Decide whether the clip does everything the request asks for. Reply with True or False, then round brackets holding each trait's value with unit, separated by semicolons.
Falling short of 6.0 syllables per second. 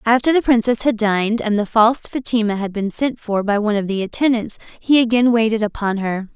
True (5.7 syllables/s)